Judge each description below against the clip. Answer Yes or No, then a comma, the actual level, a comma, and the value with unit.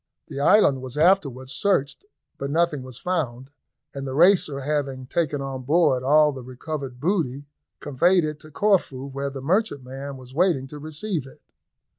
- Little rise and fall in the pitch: No, average, 3.8 semitones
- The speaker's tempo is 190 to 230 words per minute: No, average, 160 wpm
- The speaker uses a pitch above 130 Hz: Yes, medium, 140 Hz